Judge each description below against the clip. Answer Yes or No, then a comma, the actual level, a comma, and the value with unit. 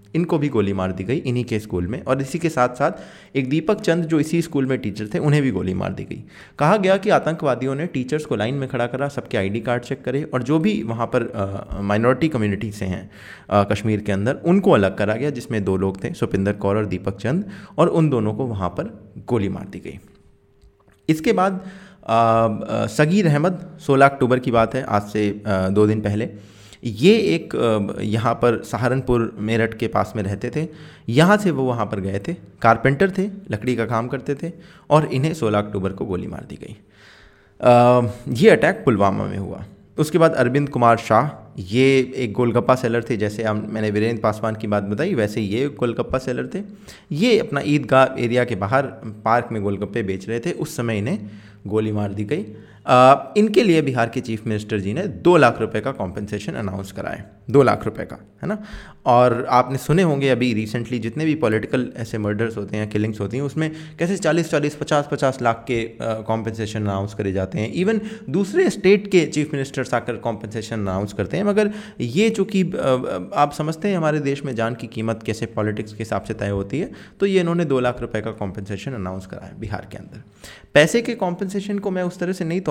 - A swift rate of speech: Yes, fast, 205 wpm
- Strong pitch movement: Yes, wide, 6.0 semitones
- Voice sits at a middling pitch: No, low, 120 Hz